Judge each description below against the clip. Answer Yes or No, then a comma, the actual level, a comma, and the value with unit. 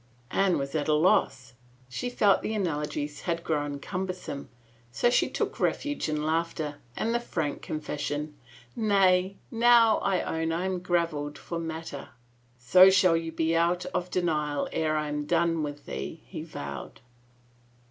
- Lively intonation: No, average, 3.7 semitones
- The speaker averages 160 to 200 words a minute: Yes, average, 175 wpm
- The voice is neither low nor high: Yes, medium, 165 Hz